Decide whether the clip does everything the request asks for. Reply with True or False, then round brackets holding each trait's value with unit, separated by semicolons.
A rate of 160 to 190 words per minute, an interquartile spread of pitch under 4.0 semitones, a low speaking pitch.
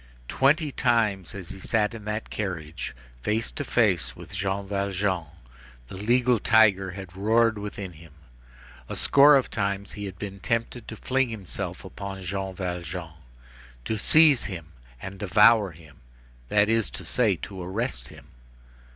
False (150 wpm; 3.3 semitones; 100 Hz)